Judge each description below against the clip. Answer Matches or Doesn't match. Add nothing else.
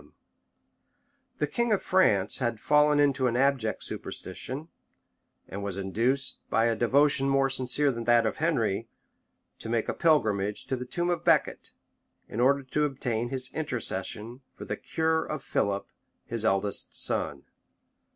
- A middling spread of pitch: Matches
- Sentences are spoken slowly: Doesn't match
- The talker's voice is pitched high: Doesn't match